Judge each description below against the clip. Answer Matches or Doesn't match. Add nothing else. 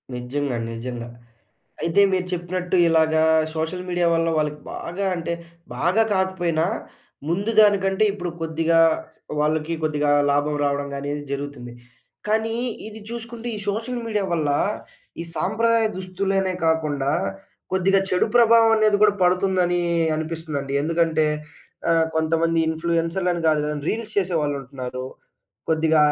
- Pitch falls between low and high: Matches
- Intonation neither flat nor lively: Matches